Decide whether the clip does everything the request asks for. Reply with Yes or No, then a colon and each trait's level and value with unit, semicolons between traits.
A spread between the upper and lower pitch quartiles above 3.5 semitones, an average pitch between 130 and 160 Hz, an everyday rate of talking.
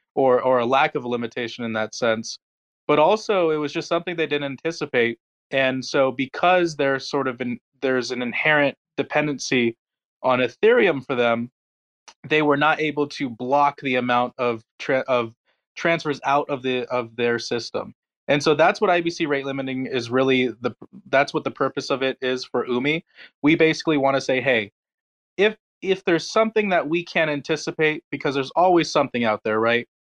Yes: average, 3.9 semitones; low, 135 Hz; average, 185 wpm